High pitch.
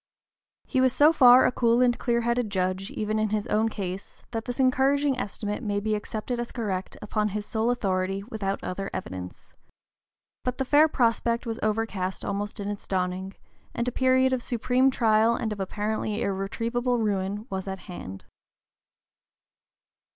Yes: high, 215 Hz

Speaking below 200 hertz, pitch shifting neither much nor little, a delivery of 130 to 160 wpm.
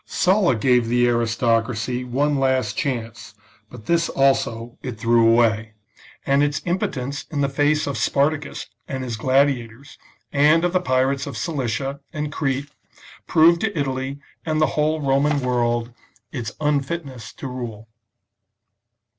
Yes: low, 135 Hz; average, 3.7 semitones; average, 140 wpm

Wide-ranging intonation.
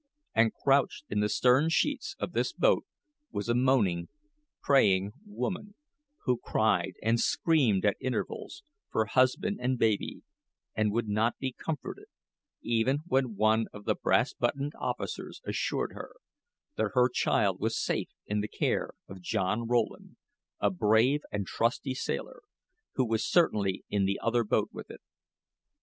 No: average, 4.2 semitones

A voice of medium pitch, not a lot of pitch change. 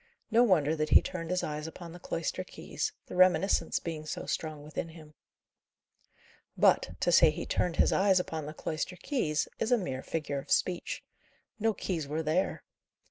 No: medium, 165 Hz; average, 3.1 semitones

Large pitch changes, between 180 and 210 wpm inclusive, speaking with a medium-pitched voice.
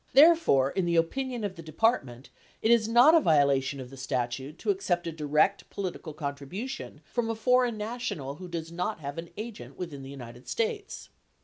Yes: wide, 8.8 semitones; average, 195 wpm; medium, 170 Hz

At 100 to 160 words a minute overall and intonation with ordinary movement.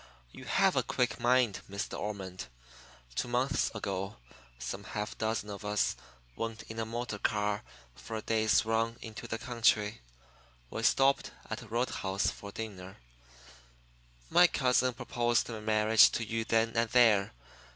No: average, 150 wpm; narrow, 2.2 semitones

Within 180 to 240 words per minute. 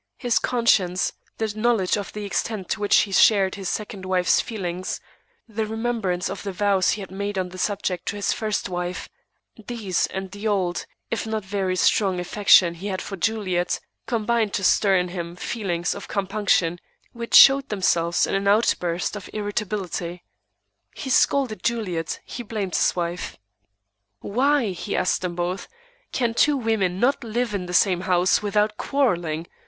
No: average, 165 wpm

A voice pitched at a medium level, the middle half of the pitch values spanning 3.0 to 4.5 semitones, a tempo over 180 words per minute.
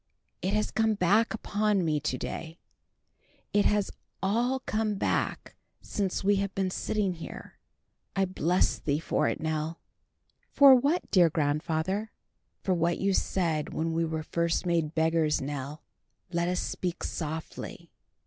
No: medium, 175 Hz; average, 4.2 semitones; average, 145 wpm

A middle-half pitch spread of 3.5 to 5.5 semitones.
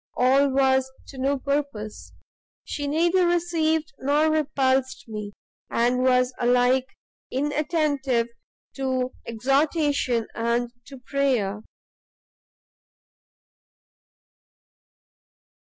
No: average, 2.8 semitones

